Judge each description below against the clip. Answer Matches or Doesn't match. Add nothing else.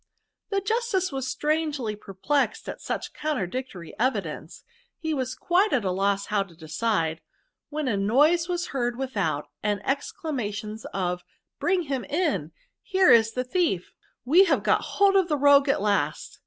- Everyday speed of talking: Matches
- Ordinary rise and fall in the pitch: Doesn't match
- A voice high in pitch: Matches